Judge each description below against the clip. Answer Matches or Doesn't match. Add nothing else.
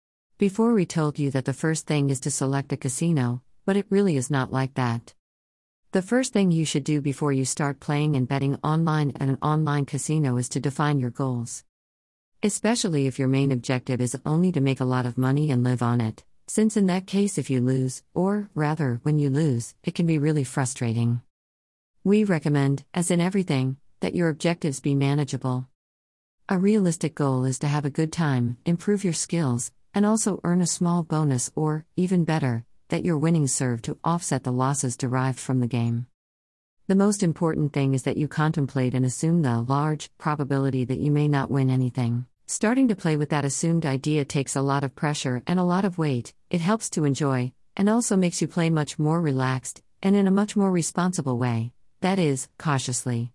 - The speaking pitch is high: Doesn't match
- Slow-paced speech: Doesn't match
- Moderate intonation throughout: Matches